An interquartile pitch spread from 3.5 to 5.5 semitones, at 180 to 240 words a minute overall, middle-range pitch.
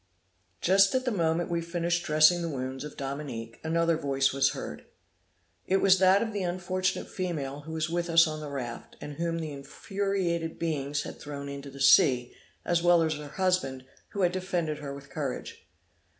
Yes: average, 3.9 semitones; average, 185 wpm; medium, 160 Hz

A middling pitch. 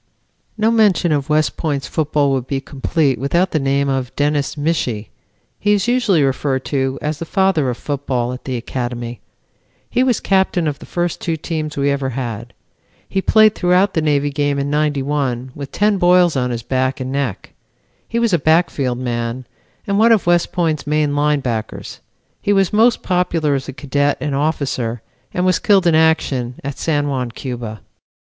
Yes: medium, 145 Hz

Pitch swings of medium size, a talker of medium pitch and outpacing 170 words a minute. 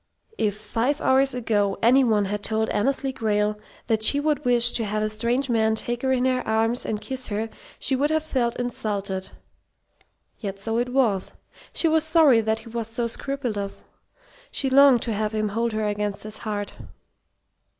No: average, 3.5 semitones; high, 230 Hz; average, 180 wpm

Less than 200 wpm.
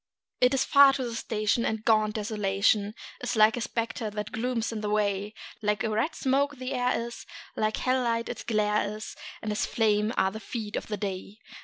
No: fast, 205 wpm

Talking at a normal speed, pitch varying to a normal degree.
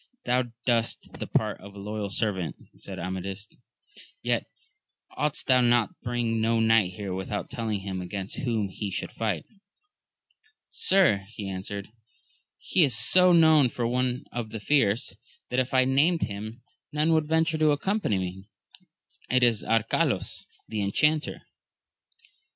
Yes: average, 150 wpm; average, 4.8 semitones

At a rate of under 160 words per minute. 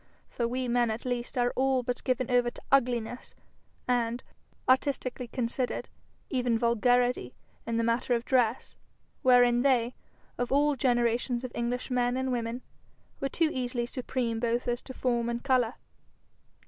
Yes: average, 150 wpm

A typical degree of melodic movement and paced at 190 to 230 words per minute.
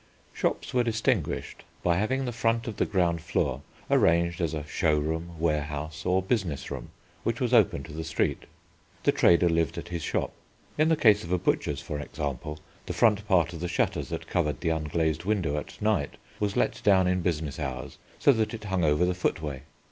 Yes: average, 4.9 semitones; average, 200 wpm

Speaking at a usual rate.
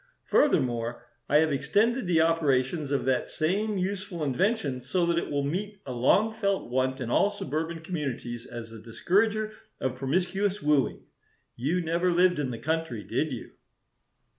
Yes: average, 160 wpm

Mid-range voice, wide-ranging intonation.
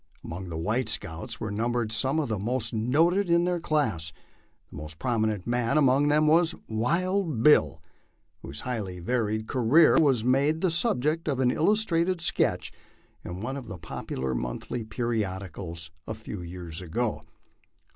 No: low, 120 Hz; wide, 7.8 semitones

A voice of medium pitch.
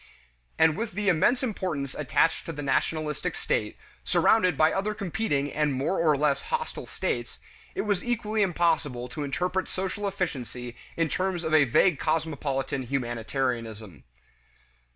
Yes: medium, 160 Hz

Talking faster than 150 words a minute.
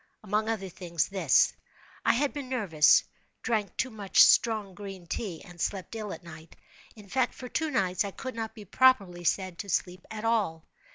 Yes: average, 175 wpm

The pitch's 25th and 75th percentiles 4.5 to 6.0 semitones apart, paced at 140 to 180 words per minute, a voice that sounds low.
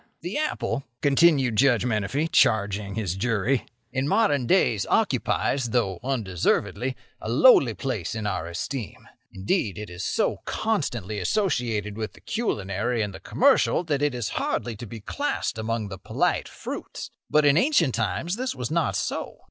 Yes: wide, 5.6 semitones; average, 155 wpm; low, 120 Hz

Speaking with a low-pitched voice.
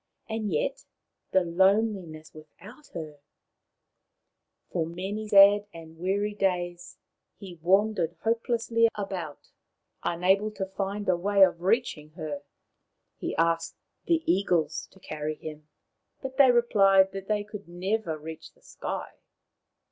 No: high, 190 Hz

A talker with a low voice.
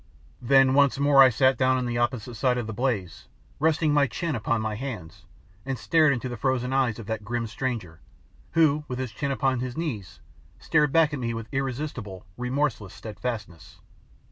Yes: low, 125 Hz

